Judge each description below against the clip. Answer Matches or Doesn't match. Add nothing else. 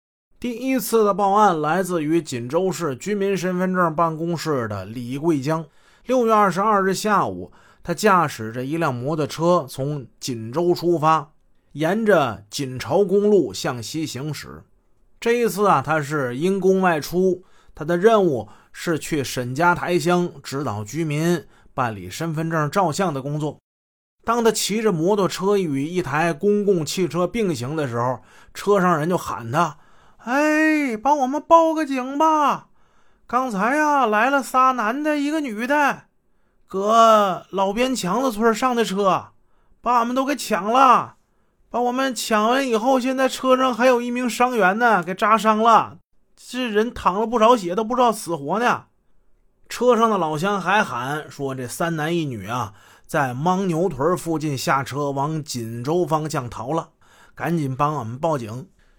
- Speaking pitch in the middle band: Matches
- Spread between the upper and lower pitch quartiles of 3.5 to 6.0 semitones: Doesn't match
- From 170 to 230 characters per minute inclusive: Matches